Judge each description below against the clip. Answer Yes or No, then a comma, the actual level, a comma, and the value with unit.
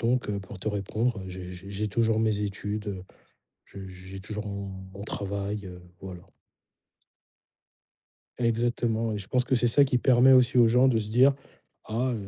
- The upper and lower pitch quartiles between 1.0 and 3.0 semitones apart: No, average, 3.4 semitones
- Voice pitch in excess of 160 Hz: No, low, 105 Hz